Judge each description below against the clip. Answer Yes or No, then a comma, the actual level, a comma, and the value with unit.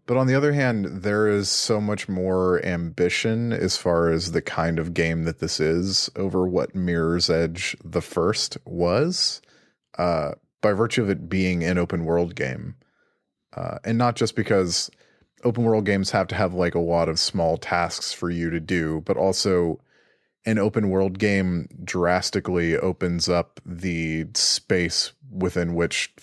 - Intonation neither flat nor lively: Yes, average, 3.4 semitones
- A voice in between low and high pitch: No, very low, 90 Hz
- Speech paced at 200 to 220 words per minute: No, average, 165 wpm